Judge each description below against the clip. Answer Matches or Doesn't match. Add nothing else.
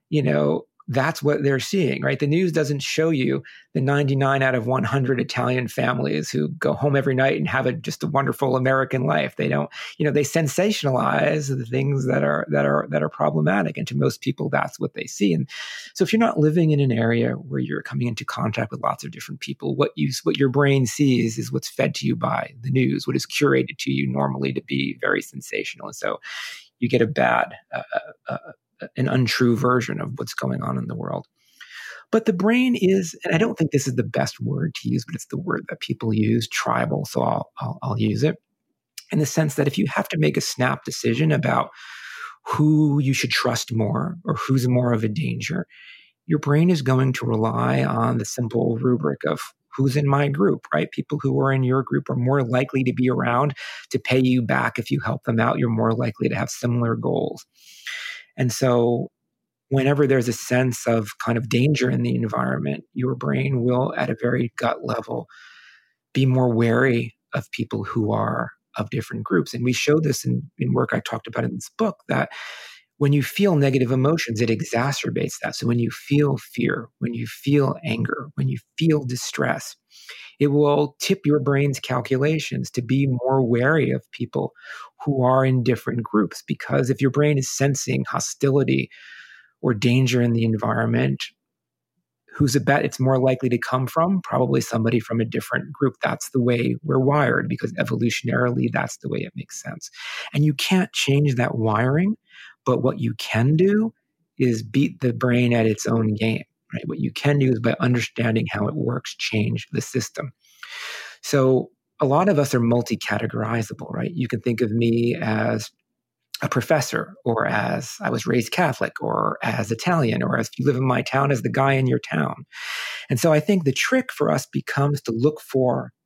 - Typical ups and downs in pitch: Matches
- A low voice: Matches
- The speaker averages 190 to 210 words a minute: Matches